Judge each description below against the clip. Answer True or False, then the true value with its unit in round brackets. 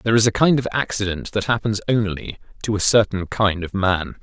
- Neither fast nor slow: False (215 wpm)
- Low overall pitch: True (105 Hz)